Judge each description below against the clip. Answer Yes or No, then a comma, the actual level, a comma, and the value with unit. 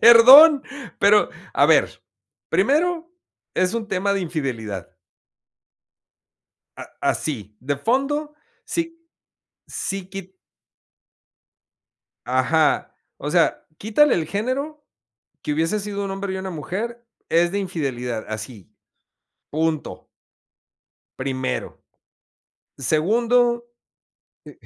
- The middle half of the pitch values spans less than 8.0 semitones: No, wide, 8.4 semitones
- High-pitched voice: Yes, high, 195 Hz